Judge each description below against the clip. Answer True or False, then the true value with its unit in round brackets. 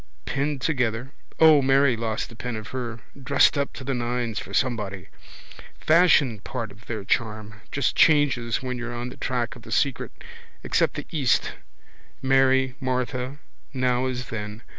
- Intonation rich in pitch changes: False (2.6 semitones)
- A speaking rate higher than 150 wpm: True (160 wpm)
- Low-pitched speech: True (125 Hz)